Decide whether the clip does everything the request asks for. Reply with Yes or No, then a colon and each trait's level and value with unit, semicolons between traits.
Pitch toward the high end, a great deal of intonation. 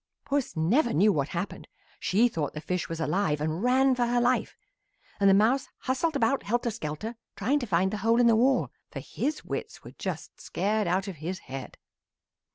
Yes: high, 215 Hz; wide, 6.0 semitones